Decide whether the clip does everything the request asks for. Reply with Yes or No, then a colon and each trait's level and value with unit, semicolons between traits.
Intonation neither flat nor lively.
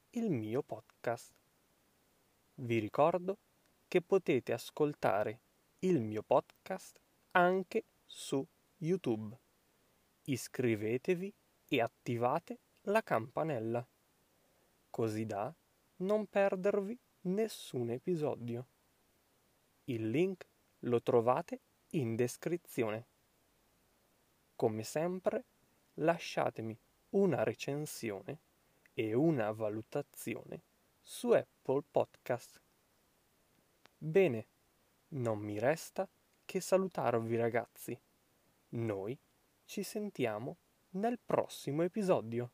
No: wide, 8.3 semitones